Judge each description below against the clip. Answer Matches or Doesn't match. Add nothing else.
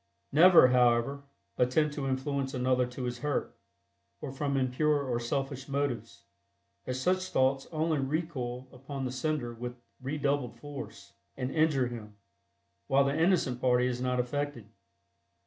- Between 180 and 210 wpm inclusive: Doesn't match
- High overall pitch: Doesn't match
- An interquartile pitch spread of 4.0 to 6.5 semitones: Doesn't match